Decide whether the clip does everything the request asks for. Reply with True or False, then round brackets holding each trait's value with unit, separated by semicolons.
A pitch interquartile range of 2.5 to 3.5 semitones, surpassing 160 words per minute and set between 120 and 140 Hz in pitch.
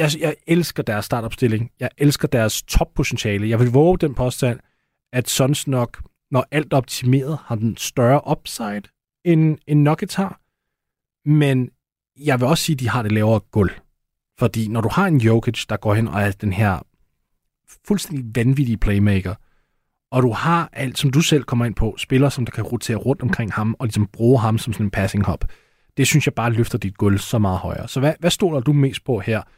False (5.0 semitones; 205 wpm; 125 Hz)